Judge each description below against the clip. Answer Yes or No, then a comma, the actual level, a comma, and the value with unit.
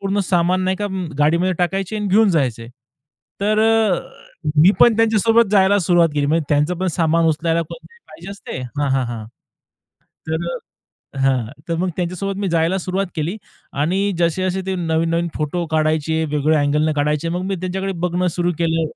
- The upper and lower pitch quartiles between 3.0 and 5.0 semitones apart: Yes, average, 3.4 semitones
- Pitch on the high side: No, medium, 170 Hz